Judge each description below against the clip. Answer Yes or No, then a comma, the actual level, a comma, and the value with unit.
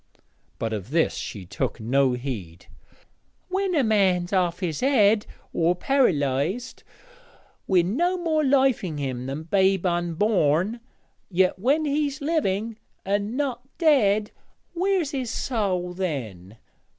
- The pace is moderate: No, slow, 125 wpm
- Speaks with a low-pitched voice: No, high, 195 Hz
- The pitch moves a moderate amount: No, wide, 8.9 semitones